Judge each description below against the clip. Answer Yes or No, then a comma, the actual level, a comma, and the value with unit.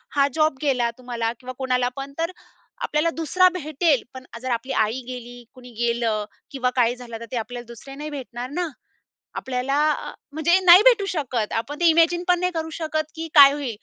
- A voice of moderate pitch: No, very high, 275 Hz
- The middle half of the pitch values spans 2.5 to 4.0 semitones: No, average, 4.4 semitones